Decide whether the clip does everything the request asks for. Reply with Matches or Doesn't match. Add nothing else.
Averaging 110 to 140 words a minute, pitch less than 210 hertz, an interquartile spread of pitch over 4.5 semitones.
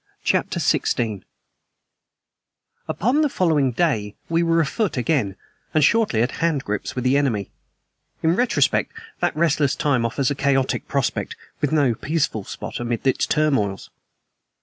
Matches